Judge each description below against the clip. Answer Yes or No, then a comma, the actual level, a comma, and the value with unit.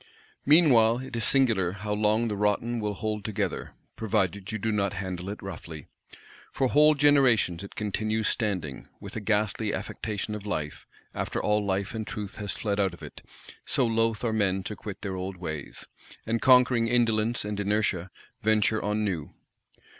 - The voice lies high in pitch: No, low, 105 Hz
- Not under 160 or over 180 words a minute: Yes, average, 170 wpm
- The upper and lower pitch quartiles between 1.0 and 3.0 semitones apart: Yes, narrow, 2.5 semitones